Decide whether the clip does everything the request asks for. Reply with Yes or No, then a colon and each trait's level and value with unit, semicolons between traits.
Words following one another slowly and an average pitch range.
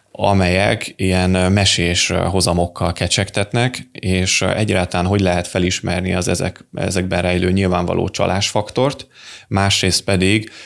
No: slow, 100 wpm; narrow, 2.1 semitones